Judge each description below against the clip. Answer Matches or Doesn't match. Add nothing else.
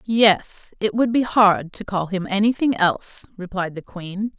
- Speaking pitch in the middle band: Doesn't match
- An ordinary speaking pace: Matches